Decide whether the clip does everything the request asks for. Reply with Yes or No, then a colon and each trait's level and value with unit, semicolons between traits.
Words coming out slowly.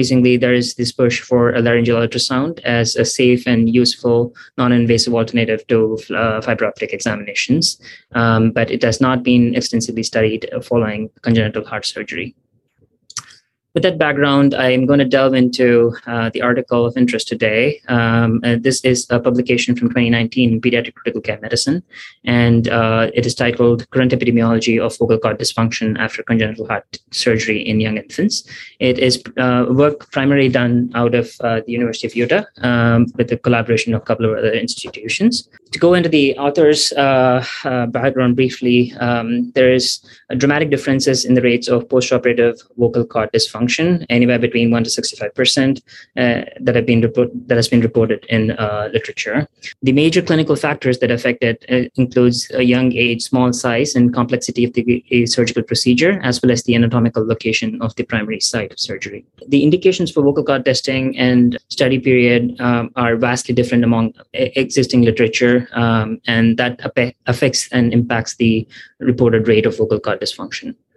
No: average, 170 wpm